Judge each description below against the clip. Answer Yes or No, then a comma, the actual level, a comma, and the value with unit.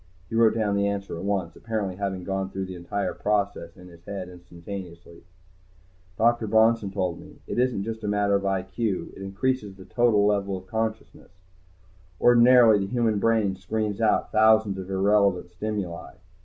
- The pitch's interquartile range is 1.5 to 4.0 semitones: Yes, narrow, 2.6 semitones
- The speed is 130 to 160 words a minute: No, average, 170 wpm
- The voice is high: No, low, 100 Hz